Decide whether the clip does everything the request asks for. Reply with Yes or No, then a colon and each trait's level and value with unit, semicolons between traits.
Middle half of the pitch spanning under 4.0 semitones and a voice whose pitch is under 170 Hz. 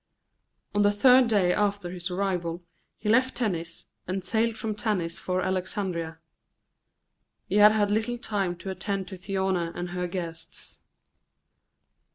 No: average, 2.9 semitones; high, 190 Hz